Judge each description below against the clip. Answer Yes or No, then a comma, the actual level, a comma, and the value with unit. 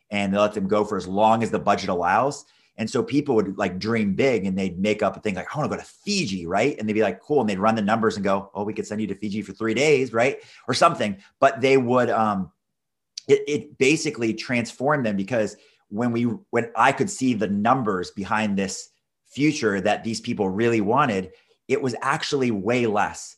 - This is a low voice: Yes, low, 110 Hz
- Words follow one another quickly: Yes, fast, 230 wpm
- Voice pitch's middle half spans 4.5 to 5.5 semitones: No, average, 3.4 semitones